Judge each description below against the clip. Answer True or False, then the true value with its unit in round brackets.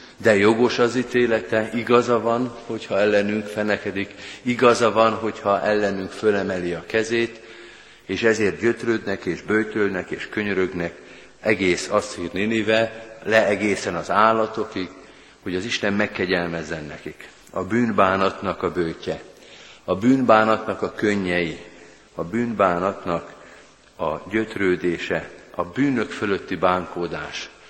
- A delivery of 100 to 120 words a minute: True (110 wpm)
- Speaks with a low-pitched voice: True (105 Hz)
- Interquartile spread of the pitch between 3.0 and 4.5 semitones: True (3.4 semitones)